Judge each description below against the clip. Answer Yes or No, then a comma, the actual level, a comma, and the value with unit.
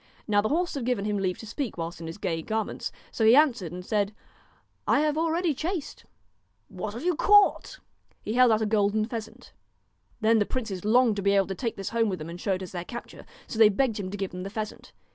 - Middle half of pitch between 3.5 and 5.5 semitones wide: Yes, average, 4.2 semitones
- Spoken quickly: Yes, fast, 255 wpm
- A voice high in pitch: Yes, high, 215 Hz